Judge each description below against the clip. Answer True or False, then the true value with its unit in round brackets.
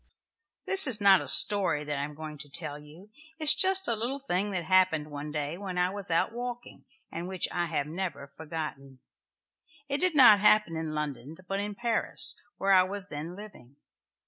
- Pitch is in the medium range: True (180 Hz)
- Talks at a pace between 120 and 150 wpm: False (200 wpm)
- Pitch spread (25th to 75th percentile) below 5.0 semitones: False (5.6 semitones)